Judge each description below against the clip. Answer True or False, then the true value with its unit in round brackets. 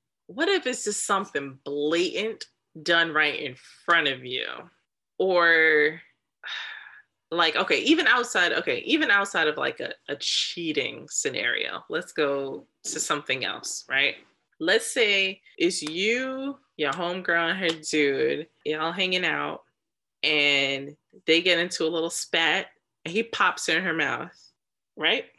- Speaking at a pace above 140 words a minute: False (135 wpm)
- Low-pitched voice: False (170 Hz)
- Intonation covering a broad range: True (8.8 semitones)